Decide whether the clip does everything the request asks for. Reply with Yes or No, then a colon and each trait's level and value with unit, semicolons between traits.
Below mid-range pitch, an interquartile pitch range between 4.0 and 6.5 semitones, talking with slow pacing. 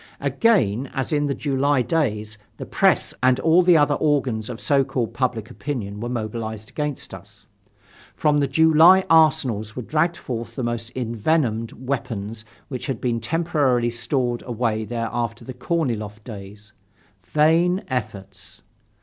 No: low, 125 Hz; average, 4.9 semitones; average, 145 wpm